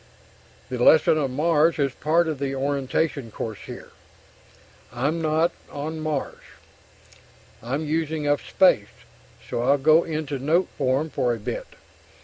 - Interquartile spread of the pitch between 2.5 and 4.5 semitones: Yes, average, 3.0 semitones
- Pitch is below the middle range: No, medium, 145 Hz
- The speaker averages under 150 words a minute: Yes, slow, 135 wpm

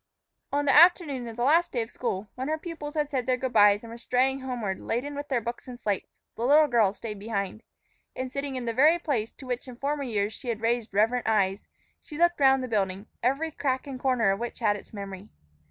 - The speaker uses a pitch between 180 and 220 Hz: No, high, 245 Hz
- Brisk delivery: Yes, fast, 235 wpm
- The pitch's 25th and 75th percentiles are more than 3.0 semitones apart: Yes, average, 4.2 semitones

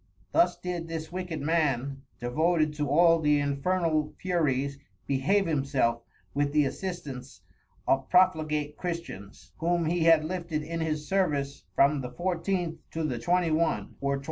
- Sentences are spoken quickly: No, average, 145 wpm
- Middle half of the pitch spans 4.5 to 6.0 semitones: No, average, 3.5 semitones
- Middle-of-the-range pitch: Yes, medium, 155 Hz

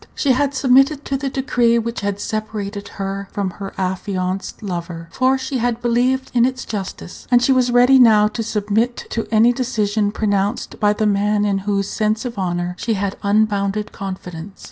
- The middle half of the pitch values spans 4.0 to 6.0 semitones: No, average, 3.6 semitones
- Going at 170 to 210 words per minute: Yes, average, 180 wpm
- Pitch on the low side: No, high, 215 Hz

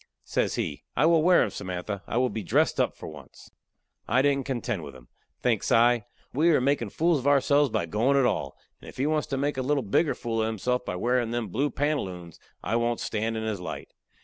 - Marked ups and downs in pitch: No, average, 4.5 semitones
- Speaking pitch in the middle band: No, low, 120 Hz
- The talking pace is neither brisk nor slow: No, fast, 230 wpm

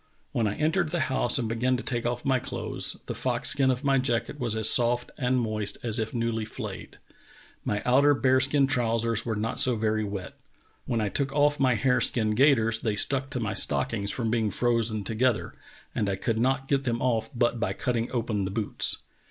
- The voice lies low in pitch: Yes, low, 120 Hz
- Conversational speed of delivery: No, fast, 210 wpm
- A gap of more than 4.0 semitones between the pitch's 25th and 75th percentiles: No, average, 2.9 semitones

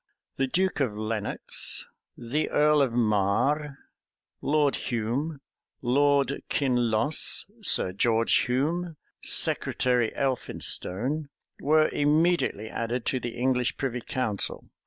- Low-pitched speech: Yes, low, 130 Hz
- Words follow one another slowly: Yes, slow, 100 wpm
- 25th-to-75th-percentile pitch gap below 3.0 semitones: No, average, 4.2 semitones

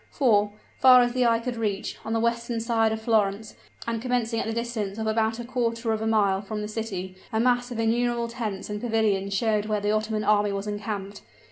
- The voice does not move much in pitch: Yes, narrow, 2.0 semitones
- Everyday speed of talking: No, fast, 220 wpm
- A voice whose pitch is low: No, high, 220 Hz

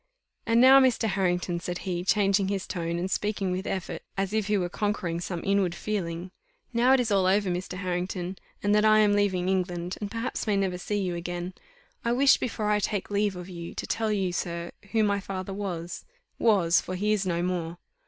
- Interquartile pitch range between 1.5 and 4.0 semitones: Yes, average, 2.8 semitones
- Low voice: No, high, 190 Hz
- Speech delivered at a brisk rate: Yes, fast, 210 wpm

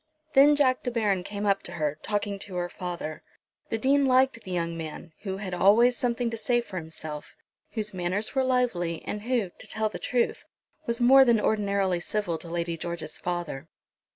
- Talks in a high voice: Yes, high, 200 Hz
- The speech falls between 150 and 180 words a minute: No, average, 190 wpm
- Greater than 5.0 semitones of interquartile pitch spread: Yes, wide, 5.4 semitones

